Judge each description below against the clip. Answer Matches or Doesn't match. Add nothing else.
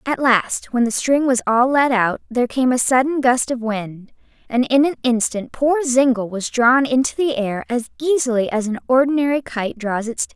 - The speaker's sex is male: Doesn't match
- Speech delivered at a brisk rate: Matches